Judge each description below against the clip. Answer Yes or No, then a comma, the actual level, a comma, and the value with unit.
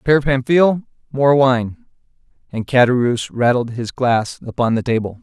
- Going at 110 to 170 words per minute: Yes, average, 140 wpm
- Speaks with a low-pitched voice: Yes, low, 130 Hz